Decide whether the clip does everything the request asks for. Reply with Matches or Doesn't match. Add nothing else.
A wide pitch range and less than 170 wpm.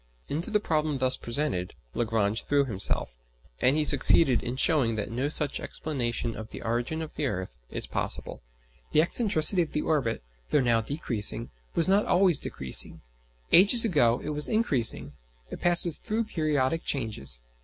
Matches